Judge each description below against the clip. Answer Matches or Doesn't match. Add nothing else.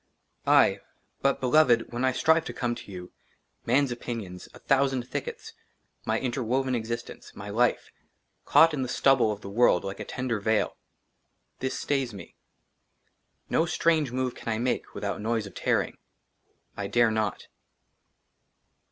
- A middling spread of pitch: Matches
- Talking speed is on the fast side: Doesn't match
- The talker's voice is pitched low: Matches